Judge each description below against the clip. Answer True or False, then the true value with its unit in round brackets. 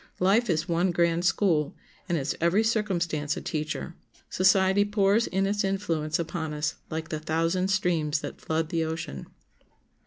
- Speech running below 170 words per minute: True (155 wpm)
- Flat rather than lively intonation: False (3.5 semitones)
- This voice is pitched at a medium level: True (170 Hz)